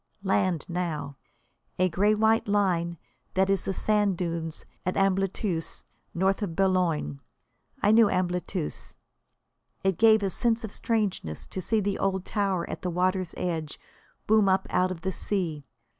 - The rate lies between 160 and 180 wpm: No, average, 150 wpm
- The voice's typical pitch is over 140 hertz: Yes, high, 190 Hz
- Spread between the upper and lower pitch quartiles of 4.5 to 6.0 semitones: No, average, 2.8 semitones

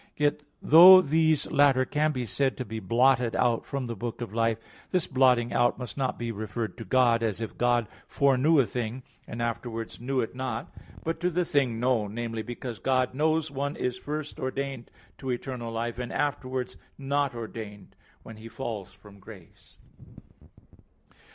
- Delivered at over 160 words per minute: Yes, average, 170 wpm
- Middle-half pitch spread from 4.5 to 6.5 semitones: No, average, 3.3 semitones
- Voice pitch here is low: Yes, low, 125 Hz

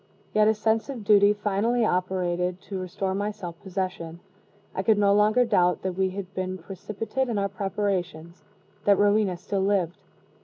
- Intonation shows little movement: Yes, narrow, 2.2 semitones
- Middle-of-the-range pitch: No, high, 195 Hz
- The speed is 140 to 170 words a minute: Yes, average, 165 wpm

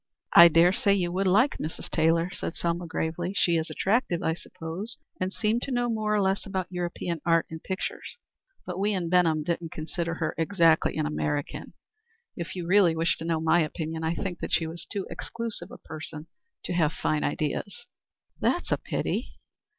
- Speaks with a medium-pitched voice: Yes, medium, 170 Hz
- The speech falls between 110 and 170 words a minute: No, average, 190 wpm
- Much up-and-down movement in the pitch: No, average, 2.9 semitones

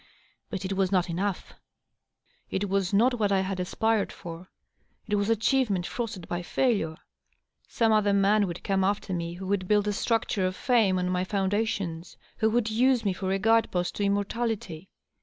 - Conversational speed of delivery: Yes, average, 180 wpm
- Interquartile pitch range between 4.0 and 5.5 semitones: No, average, 2.9 semitones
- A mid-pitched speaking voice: No, high, 200 Hz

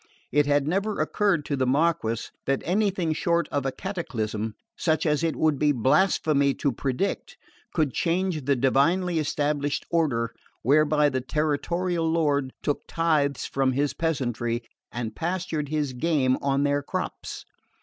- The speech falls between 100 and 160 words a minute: Yes, average, 145 wpm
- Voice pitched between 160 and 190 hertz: No, medium, 145 Hz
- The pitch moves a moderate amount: Yes, average, 3.6 semitones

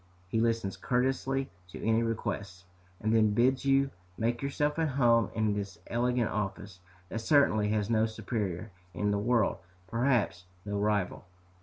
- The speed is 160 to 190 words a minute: No, average, 150 wpm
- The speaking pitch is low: Yes, low, 110 Hz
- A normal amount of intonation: Yes, average, 3.3 semitones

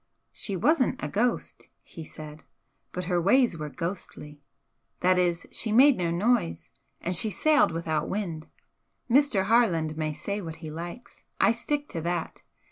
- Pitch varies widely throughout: Yes, wide, 6.2 semitones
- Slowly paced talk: No, average, 155 wpm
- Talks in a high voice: No, medium, 180 Hz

